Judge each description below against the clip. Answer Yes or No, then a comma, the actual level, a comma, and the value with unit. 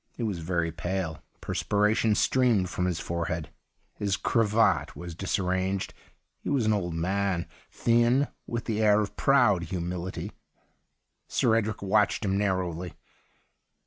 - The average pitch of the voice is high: No, low, 100 Hz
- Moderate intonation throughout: Yes, average, 3.7 semitones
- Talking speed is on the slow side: Yes, slow, 130 wpm